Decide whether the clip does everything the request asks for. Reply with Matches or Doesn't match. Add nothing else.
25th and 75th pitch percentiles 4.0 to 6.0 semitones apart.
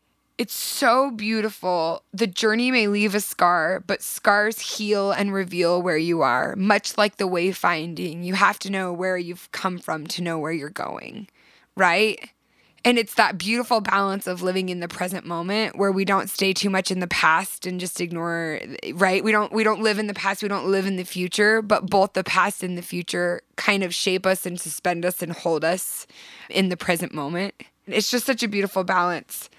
Doesn't match